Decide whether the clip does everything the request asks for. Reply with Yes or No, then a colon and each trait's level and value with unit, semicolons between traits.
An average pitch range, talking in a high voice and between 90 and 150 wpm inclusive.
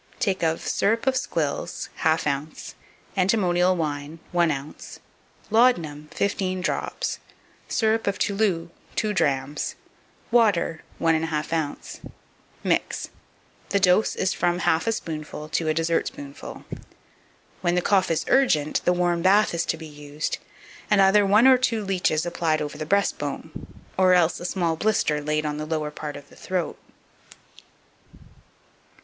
No: average, 4.3 semitones; medium, 170 Hz; average, 145 wpm